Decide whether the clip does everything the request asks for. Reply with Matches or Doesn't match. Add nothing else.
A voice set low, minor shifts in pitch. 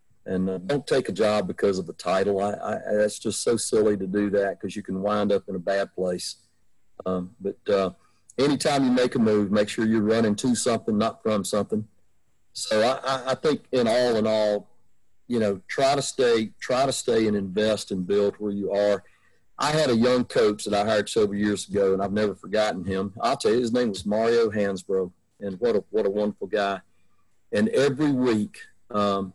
Matches